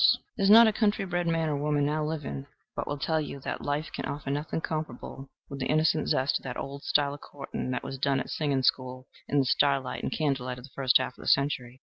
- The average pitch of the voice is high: No, medium, 140 Hz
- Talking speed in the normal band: No, fast, 250 wpm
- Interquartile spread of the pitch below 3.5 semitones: Yes, average, 2.7 semitones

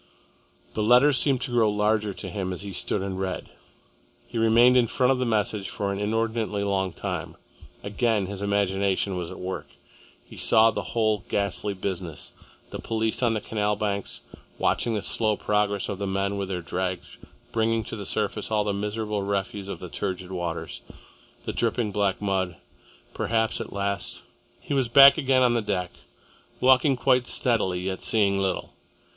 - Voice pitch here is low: Yes, low, 105 Hz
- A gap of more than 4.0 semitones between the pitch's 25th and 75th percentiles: No, average, 2.7 semitones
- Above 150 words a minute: Yes, average, 175 wpm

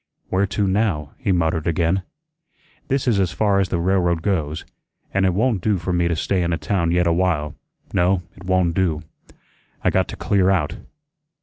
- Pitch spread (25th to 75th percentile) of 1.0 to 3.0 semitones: Yes, narrow, 2.5 semitones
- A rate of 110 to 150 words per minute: No, average, 195 wpm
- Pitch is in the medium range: No, very low, 90 Hz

